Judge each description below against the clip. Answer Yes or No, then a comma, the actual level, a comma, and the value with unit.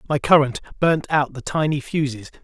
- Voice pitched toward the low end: No, medium, 145 Hz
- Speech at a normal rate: Yes, average, 170 wpm